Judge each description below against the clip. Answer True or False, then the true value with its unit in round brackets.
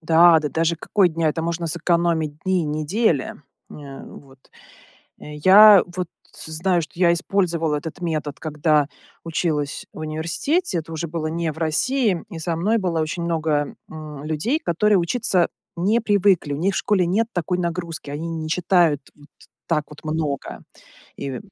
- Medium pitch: True (165 Hz)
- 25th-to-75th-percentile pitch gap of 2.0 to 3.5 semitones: True (2.7 semitones)